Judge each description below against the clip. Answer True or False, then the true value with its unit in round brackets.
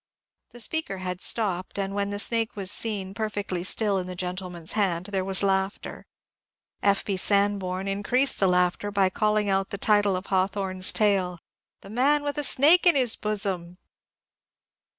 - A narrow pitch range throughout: True (2.3 semitones)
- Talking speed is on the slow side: False (170 wpm)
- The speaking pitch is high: True (200 Hz)